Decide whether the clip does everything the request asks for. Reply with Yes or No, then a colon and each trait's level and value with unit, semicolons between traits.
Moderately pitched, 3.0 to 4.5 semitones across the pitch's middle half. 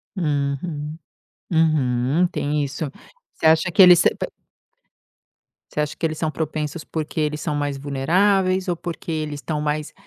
No: medium, 155 Hz; narrow, 2.4 semitones